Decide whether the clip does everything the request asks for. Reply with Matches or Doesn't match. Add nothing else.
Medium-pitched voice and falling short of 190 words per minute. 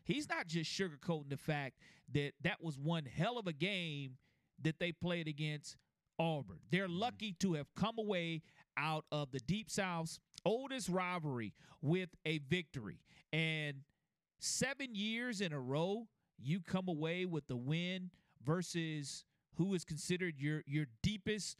Matches